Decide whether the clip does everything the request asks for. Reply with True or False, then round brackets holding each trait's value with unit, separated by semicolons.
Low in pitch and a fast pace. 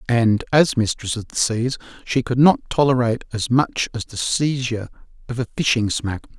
False (120 Hz; 180 wpm)